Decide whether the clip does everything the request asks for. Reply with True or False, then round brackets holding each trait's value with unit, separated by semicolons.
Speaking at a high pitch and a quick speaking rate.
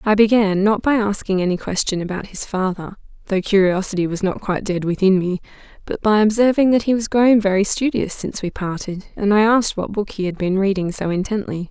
True (200 Hz; 210 wpm)